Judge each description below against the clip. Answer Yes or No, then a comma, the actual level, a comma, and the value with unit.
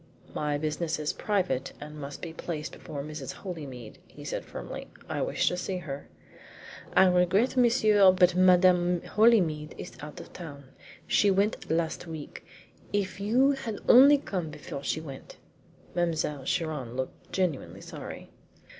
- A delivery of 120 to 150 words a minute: Yes, average, 145 wpm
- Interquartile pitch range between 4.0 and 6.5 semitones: Yes, average, 4.3 semitones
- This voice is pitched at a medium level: Yes, medium, 170 Hz